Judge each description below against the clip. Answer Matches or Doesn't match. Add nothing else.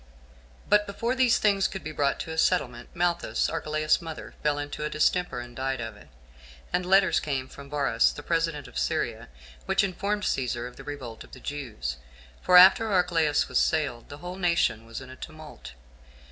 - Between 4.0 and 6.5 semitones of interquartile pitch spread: Matches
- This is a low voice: Doesn't match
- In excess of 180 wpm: Matches